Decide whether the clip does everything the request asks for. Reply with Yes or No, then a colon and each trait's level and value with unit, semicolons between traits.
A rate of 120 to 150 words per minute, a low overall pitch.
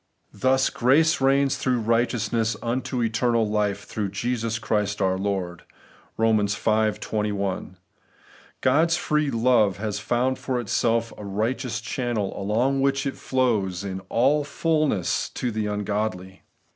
Yes: average, 140 wpm; low, 115 Hz